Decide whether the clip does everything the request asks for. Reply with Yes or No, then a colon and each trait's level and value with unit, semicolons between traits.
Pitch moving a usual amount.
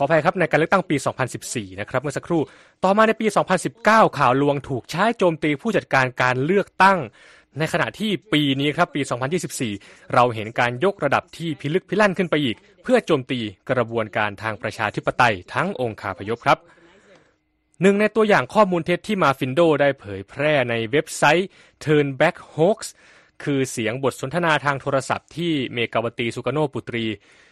No: wide, 6.0 semitones